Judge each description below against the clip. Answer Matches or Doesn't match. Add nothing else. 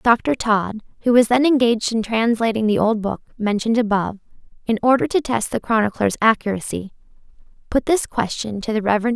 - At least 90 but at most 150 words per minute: Doesn't match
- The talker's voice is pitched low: Doesn't match